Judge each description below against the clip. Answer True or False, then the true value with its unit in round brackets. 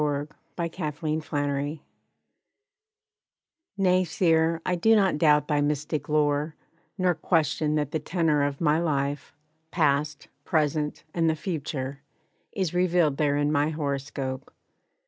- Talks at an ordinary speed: False (125 wpm)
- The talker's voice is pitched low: False (150 Hz)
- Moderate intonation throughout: False (2.3 semitones)